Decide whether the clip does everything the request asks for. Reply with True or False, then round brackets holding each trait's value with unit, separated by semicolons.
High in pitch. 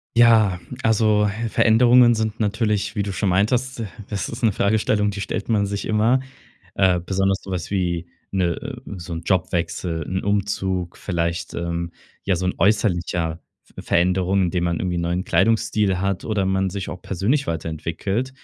False (95 Hz)